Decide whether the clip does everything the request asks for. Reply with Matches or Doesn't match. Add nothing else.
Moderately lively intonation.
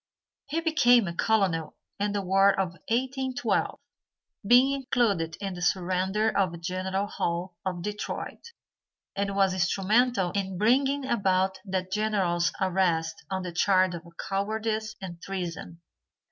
Matches